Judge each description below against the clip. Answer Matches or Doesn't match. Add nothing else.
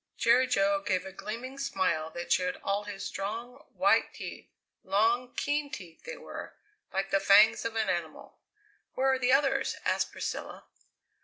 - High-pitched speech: Matches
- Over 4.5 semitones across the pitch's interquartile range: Matches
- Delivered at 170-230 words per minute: Doesn't match